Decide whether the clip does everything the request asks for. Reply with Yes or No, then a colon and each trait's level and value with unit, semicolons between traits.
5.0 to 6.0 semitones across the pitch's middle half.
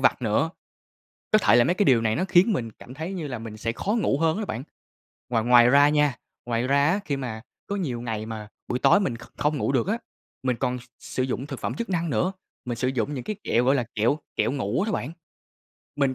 Yes: average, 5.3 semitones